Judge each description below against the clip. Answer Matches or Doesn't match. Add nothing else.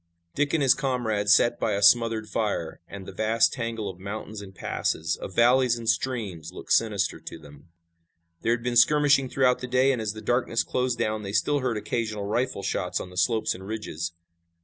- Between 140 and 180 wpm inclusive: Doesn't match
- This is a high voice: Doesn't match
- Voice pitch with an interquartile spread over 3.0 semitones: Matches